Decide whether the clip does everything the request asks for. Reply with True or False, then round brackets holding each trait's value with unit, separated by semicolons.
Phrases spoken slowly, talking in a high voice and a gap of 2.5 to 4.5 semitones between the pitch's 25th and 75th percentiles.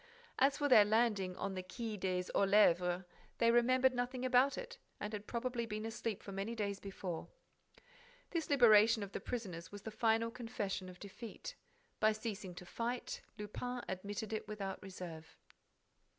False (160 wpm; 215 Hz; 3.6 semitones)